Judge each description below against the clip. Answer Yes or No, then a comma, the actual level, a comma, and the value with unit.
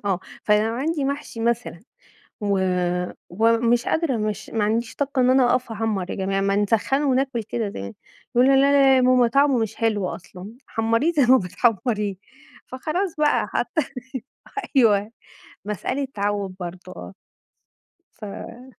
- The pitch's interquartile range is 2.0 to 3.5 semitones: No, average, 4.4 semitones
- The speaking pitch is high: Yes, high, 230 Hz